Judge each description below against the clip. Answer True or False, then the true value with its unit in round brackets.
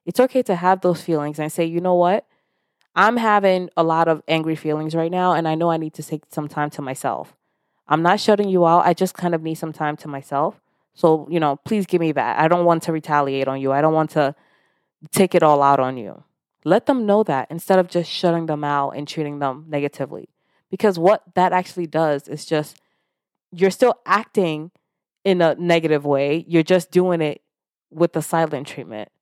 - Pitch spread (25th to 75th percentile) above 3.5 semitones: False (3.2 semitones)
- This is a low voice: False (165 Hz)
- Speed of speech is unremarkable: False (215 wpm)